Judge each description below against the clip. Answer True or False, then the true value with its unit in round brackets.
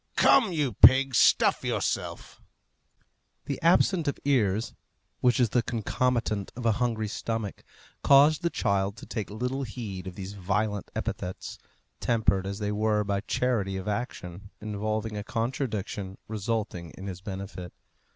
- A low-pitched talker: True (110 Hz)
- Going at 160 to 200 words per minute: False (140 wpm)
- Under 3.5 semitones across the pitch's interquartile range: False (3.9 semitones)